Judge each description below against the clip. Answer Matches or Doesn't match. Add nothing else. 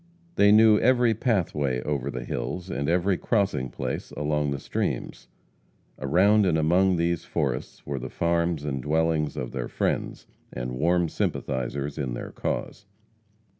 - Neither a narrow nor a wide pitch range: Matches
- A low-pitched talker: Matches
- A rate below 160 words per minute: Matches